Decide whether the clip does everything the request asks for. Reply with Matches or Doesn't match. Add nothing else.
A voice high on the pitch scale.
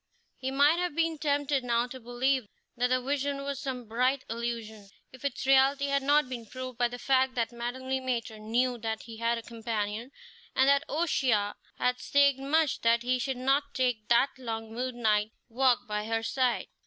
Matches